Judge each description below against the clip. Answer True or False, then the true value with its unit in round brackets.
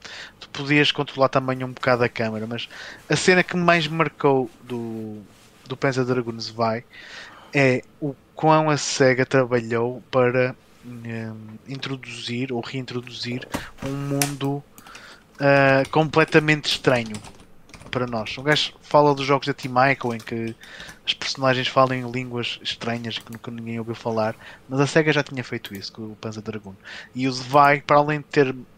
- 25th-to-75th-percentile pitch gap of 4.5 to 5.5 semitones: False (3.3 semitones)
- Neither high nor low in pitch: False (130 Hz)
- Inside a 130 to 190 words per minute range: True (160 wpm)